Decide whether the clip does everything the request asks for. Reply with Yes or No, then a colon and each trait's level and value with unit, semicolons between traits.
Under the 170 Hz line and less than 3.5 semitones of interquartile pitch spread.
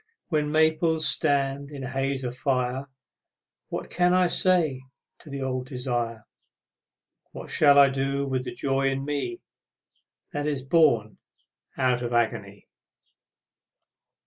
Yes: low, 135 Hz; narrow, 2.5 semitones